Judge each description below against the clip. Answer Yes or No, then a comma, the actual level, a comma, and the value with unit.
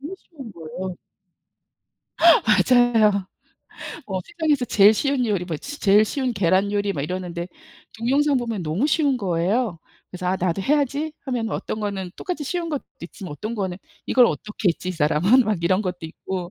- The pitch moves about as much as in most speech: No, wide, 6.1 semitones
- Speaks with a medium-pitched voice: No, high, 210 Hz